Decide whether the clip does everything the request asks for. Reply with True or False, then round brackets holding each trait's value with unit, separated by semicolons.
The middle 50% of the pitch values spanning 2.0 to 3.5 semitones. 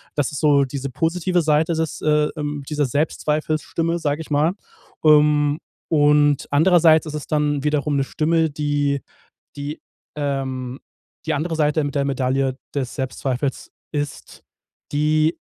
False (1.6 semitones)